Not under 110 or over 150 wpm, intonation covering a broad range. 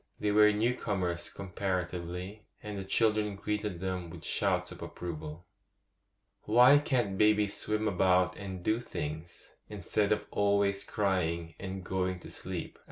No: average, 140 wpm; average, 2.8 semitones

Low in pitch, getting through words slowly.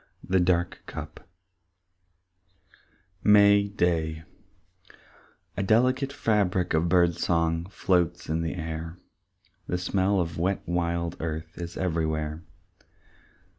Yes: very low, 85 Hz; slow, 105 wpm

